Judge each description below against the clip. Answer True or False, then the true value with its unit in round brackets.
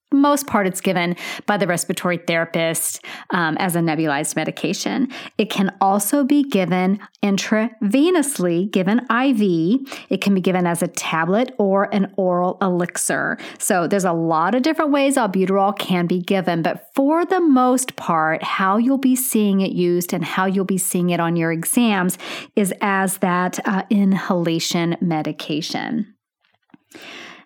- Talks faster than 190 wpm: False (150 wpm)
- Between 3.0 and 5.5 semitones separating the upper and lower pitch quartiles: True (4.2 semitones)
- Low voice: False (195 Hz)